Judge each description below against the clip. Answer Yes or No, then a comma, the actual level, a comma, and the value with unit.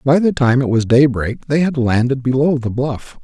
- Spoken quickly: Yes, fast, 220 wpm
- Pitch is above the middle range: No, low, 130 Hz